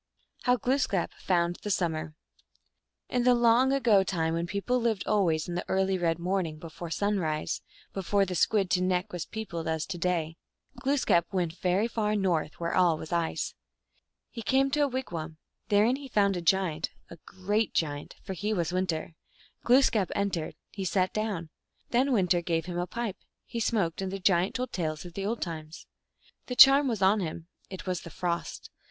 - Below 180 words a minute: No, average, 185 wpm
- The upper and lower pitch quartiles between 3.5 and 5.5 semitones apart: Yes, average, 4.3 semitones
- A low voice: No, medium, 185 Hz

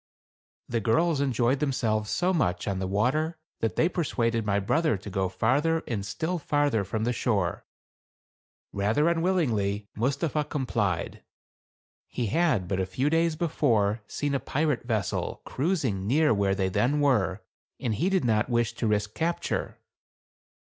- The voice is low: Yes, low, 120 Hz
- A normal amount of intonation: No, wide, 6.8 semitones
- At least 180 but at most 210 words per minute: No, average, 155 wpm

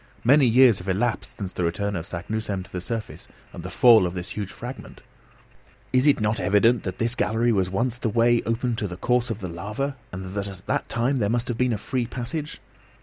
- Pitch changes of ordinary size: Yes, average, 4.2 semitones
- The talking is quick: Yes, fast, 225 wpm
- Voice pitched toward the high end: No, low, 110 Hz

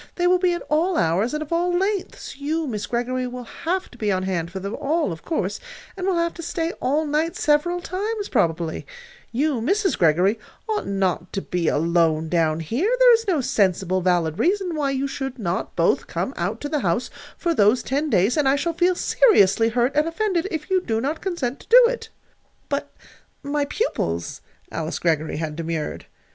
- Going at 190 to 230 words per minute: Yes, average, 200 wpm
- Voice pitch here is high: Yes, very high, 275 Hz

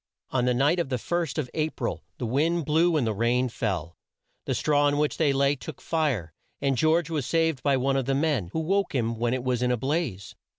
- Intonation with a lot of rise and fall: No, average, 4.3 semitones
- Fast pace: Yes, fast, 240 wpm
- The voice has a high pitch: No, medium, 140 Hz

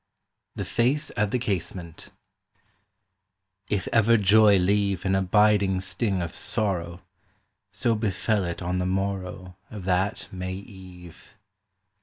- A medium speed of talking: No, slow, 120 wpm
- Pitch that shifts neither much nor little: No, narrow, 2.3 semitones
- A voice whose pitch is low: Yes, very low, 95 Hz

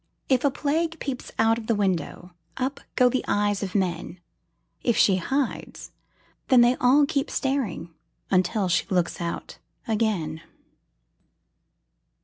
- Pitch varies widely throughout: Yes, wide, 6.2 semitones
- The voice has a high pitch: Yes, high, 225 Hz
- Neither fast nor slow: No, slow, 130 wpm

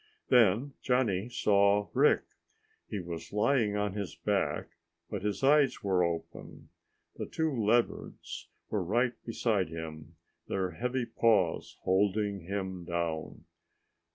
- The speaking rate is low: Yes, slow, 120 wpm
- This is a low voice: Yes, low, 100 Hz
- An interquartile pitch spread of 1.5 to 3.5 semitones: No, average, 4.2 semitones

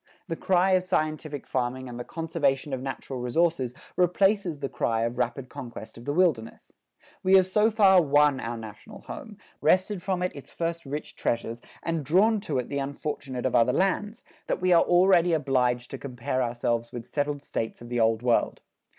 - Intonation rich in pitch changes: Yes, wide, 6.3 semitones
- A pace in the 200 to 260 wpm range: No, average, 185 wpm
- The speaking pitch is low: No, medium, 145 Hz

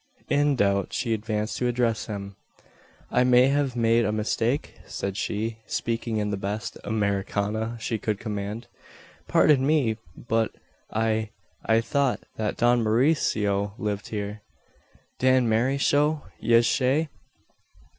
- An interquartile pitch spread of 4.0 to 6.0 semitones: No, average, 3.0 semitones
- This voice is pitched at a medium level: No, low, 115 Hz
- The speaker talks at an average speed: No, slow, 125 wpm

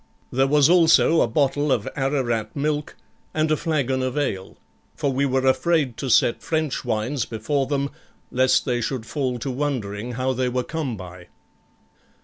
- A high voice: No, low, 130 Hz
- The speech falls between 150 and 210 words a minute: Yes, average, 165 wpm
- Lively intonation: No, average, 3.2 semitones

